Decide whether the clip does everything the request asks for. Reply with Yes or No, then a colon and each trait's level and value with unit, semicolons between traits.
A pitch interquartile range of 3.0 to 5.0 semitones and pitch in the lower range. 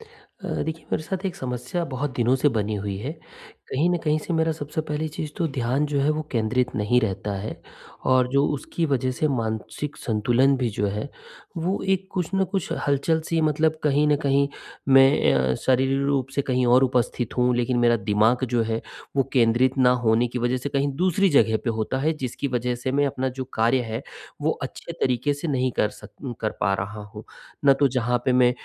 Yes: average, 3.7 semitones; low, 130 Hz